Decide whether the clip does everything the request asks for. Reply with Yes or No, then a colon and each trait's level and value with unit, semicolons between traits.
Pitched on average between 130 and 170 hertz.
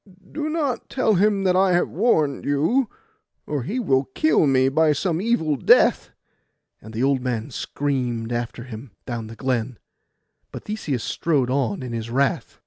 Yes: medium, 140 Hz